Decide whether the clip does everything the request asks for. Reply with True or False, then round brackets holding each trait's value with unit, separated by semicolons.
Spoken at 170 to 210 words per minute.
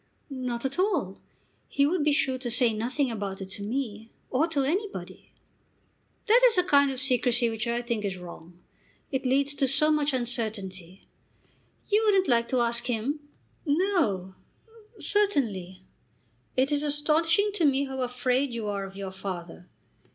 False (160 wpm)